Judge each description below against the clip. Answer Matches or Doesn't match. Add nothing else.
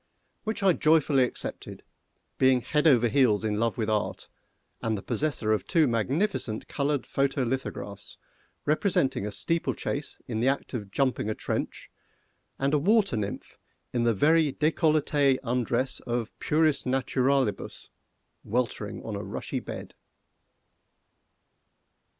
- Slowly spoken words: Matches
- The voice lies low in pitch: Matches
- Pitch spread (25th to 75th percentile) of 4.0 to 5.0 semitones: Matches